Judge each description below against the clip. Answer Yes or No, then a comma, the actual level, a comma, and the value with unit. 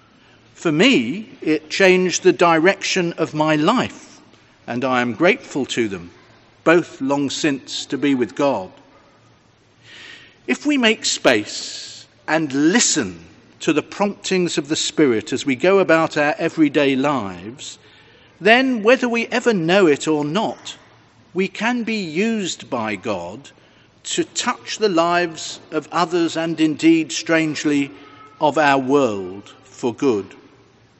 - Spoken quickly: No, slow, 135 wpm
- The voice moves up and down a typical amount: No, wide, 6.1 semitones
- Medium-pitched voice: Yes, medium, 160 Hz